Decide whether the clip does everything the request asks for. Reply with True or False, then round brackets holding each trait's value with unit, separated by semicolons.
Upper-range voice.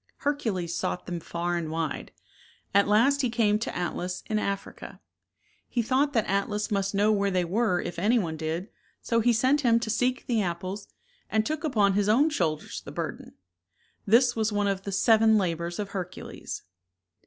True (205 Hz)